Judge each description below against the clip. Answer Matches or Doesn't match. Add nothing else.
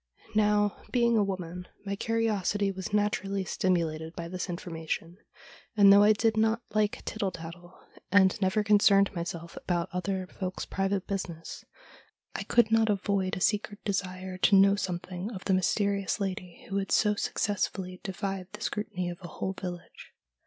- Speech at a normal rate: Matches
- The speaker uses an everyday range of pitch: Doesn't match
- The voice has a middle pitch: Doesn't match